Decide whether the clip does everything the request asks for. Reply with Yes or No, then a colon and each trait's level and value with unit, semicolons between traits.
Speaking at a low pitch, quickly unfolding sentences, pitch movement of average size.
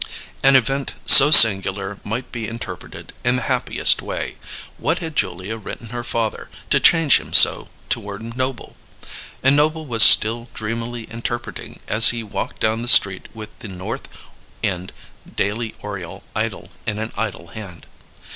No: low, 115 Hz; average, 150 wpm; average, 3.1 semitones